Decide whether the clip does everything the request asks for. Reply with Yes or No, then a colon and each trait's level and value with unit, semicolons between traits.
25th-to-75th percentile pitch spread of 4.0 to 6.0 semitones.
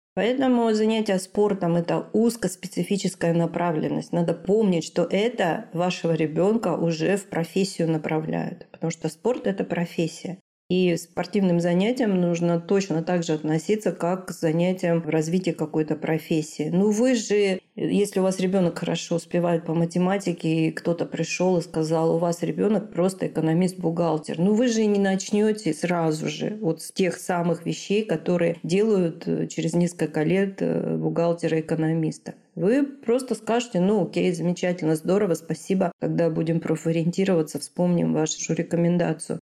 No: average, 2.8 semitones